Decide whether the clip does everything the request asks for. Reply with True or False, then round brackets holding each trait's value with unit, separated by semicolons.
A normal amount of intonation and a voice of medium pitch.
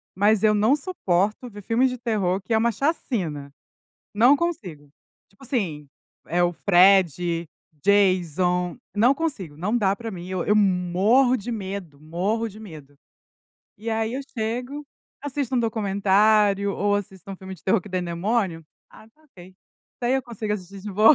False (4.2 semitones; 200 Hz)